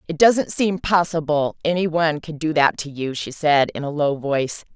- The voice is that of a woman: Yes, female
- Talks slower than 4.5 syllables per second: No, 5.0 syllables/s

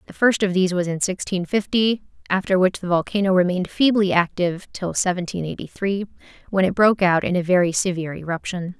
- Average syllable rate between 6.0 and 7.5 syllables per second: Yes, 6.1 syllables/s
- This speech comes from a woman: Yes, female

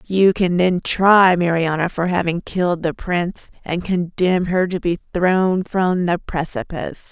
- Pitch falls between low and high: Yes, medium, 180 Hz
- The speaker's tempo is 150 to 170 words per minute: Yes, average, 160 wpm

